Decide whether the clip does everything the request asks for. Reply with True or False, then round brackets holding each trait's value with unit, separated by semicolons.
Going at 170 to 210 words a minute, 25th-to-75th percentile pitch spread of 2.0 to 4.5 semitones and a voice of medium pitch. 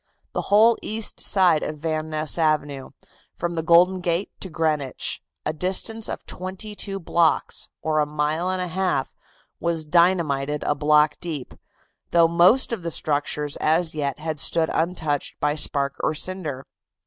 False (160 wpm; 3.3 semitones; 160 Hz)